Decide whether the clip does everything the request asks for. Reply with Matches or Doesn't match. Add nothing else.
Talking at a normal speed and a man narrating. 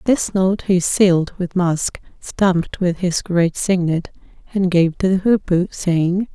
Doesn't match